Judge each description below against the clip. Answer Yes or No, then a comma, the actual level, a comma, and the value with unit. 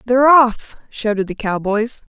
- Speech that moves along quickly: No, average, 140 wpm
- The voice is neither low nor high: No, high, 230 Hz